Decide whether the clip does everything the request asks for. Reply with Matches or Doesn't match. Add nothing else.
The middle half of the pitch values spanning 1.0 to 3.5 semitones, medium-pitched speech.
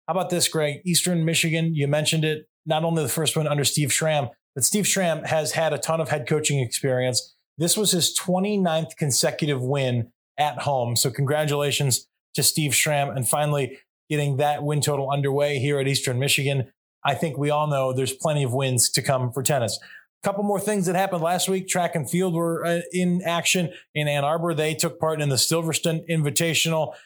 Matches